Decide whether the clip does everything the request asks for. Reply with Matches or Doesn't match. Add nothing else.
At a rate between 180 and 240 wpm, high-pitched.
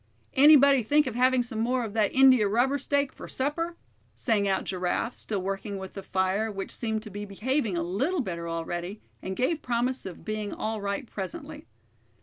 Matches